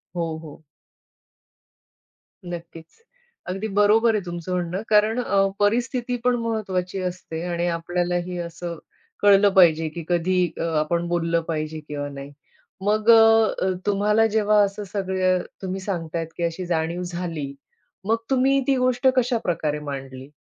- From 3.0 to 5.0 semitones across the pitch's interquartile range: Yes, average, 4.0 semitones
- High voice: No, medium, 180 Hz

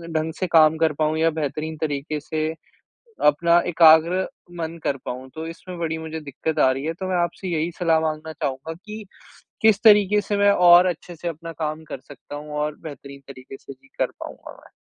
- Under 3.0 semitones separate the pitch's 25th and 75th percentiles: Yes, narrow, 2.4 semitones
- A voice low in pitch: No, medium, 160 Hz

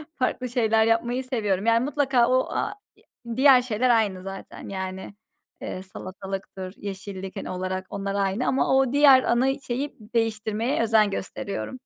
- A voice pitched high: Yes, high, 225 Hz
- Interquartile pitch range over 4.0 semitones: Yes, average, 4.7 semitones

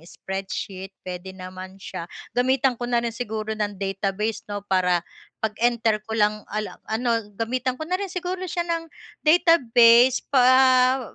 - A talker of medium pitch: No, high, 225 Hz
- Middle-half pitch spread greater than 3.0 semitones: Yes, average, 4.5 semitones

